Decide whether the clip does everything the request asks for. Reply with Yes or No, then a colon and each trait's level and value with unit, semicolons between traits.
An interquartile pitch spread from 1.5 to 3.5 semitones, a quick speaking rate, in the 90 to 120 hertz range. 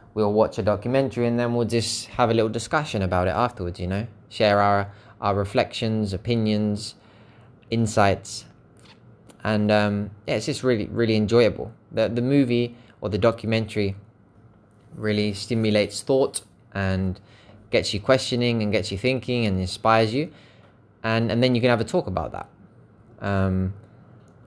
No: narrow, 2.5 semitones; average, 150 wpm; low, 110 Hz